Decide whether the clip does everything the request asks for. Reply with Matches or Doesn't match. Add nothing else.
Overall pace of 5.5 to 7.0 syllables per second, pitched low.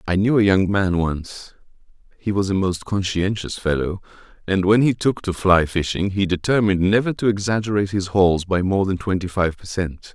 Doesn't match